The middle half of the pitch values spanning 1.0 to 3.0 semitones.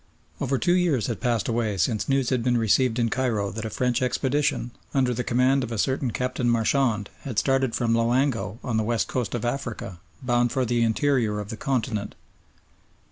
Yes: average, 2.7 semitones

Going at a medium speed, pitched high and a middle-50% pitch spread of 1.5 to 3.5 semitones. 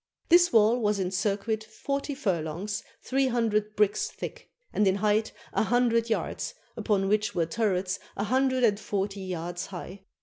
Yes: average, 160 wpm; high, 210 Hz; average, 3.2 semitones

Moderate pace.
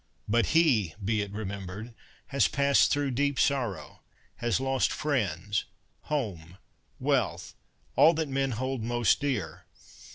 No: slow, 130 wpm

